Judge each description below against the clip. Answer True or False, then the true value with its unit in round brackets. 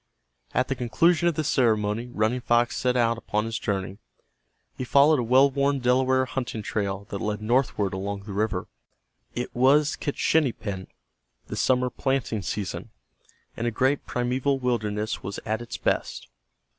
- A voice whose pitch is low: True (120 Hz)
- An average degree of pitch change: True (3.7 semitones)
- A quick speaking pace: False (155 wpm)